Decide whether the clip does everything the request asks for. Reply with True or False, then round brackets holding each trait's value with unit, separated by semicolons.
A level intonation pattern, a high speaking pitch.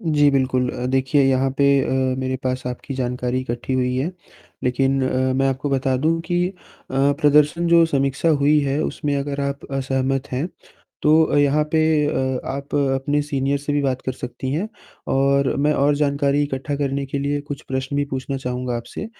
False (1.8 semitones; 140 Hz)